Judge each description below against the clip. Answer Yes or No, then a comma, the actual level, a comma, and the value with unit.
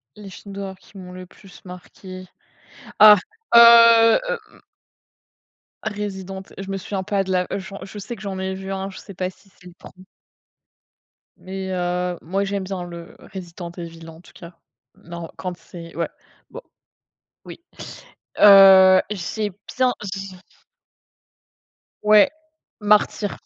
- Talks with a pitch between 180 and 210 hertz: Yes, high, 190 Hz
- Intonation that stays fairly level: Yes, narrow, 1.9 semitones